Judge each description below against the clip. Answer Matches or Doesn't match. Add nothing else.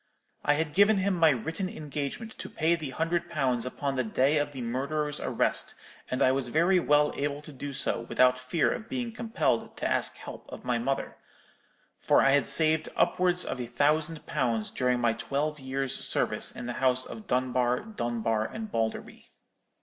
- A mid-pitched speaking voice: Matches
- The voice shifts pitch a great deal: Doesn't match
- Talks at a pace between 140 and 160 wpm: Doesn't match